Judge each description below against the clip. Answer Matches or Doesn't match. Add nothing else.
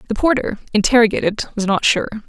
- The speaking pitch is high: Matches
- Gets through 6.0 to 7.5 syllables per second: Matches